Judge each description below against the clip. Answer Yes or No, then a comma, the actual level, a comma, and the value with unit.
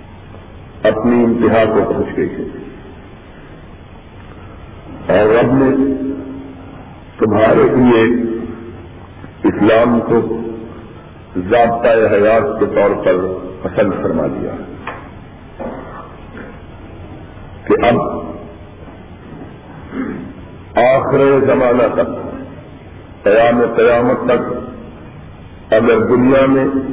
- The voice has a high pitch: No, low, 110 Hz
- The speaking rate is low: Yes, slow, 70 wpm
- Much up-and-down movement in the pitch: No, average, 4.2 semitones